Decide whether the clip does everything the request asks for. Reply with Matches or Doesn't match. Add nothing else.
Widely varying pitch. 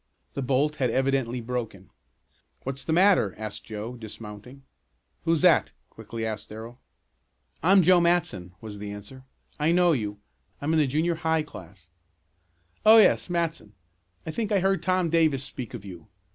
Matches